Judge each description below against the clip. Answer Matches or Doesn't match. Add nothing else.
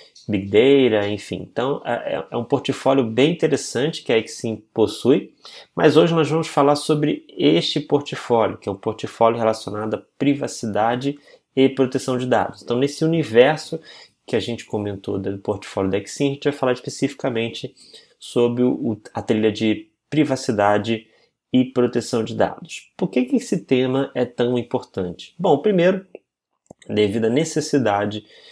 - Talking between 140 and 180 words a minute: Matches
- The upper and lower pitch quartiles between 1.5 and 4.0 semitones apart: Doesn't match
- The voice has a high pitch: Doesn't match